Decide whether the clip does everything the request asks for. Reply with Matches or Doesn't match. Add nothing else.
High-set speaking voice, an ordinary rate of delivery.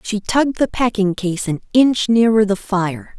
Matches